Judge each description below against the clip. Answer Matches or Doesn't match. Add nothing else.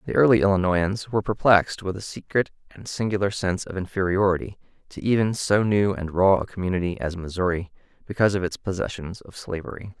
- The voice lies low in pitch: Matches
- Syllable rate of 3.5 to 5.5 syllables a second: Doesn't match